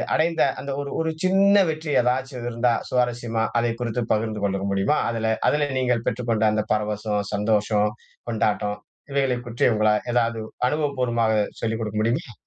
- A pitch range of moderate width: Yes, average, 3.1 semitones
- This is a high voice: No, low, 115 Hz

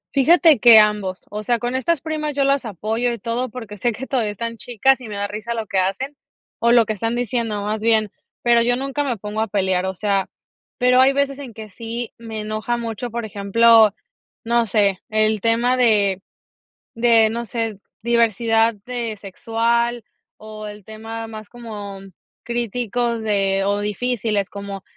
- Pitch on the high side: Yes, high, 225 Hz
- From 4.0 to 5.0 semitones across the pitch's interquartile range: No, narrow, 2.4 semitones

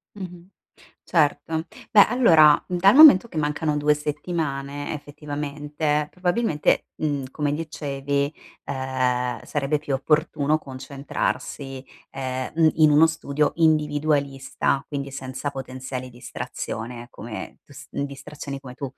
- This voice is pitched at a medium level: Yes, medium, 145 Hz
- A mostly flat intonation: Yes, narrow, 2.3 semitones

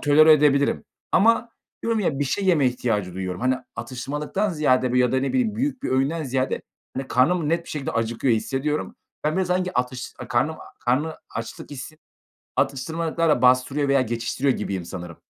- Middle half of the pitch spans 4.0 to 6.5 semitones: Yes, average, 4.4 semitones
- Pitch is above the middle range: No, medium, 140 Hz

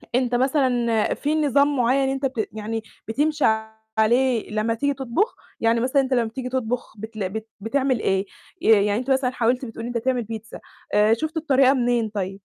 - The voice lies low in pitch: No, high, 245 Hz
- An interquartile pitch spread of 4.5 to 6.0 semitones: No, average, 3.2 semitones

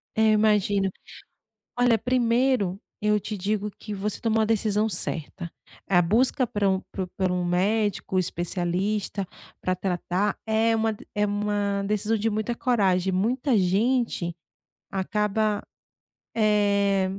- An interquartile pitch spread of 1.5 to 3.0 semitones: Yes, narrow, 2.5 semitones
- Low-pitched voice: No, high, 205 Hz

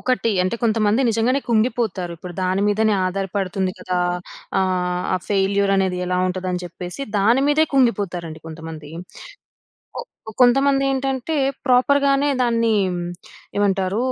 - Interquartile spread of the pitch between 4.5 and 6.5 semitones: Yes, average, 5.0 semitones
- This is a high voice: Yes, high, 200 Hz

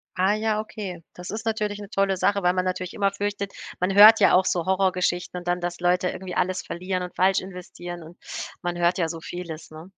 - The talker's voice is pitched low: No, medium, 185 Hz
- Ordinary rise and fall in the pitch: No, narrow, 2.0 semitones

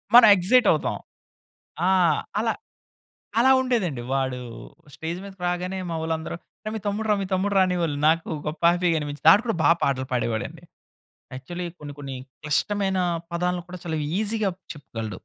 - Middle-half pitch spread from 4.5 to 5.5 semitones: Yes, average, 4.9 semitones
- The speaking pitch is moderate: Yes, medium, 175 Hz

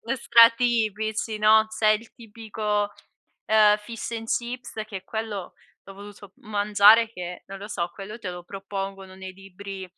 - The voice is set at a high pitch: Yes, high, 210 Hz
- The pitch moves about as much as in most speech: No, narrow, 2.1 semitones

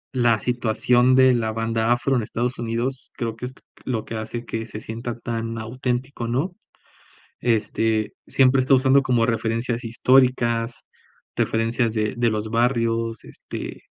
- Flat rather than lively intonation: Yes, narrow, 1.8 semitones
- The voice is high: No, low, 115 Hz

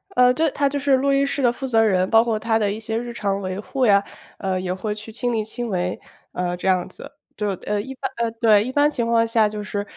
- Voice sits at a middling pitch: No, high, 225 Hz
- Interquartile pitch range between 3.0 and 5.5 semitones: Yes, average, 3.5 semitones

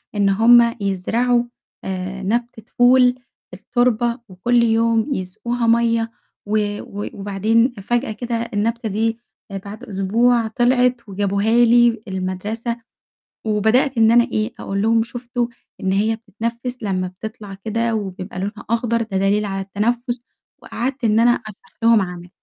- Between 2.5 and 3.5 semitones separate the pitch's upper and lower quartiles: Yes, average, 3.0 semitones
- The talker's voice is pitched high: Yes, high, 225 Hz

